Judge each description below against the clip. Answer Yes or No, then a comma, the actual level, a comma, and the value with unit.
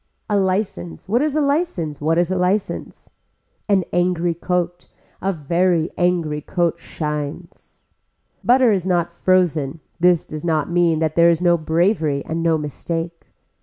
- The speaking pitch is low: No, medium, 170 Hz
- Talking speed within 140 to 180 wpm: Yes, average, 150 wpm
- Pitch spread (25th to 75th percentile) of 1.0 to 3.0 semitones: Yes, narrow, 2.6 semitones